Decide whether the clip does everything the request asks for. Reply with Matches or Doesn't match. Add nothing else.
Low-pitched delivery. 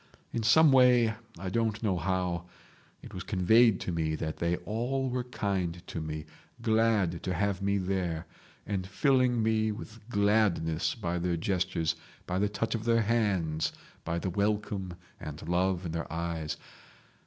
Matches